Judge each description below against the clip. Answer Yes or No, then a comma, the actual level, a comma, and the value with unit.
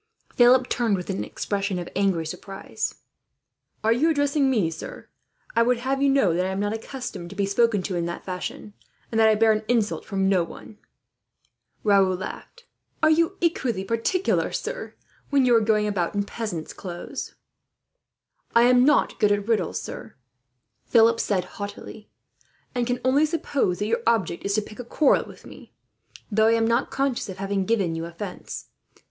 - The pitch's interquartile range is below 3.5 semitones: No, average, 4.3 semitones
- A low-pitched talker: No, high, 215 Hz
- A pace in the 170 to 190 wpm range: Yes, average, 180 wpm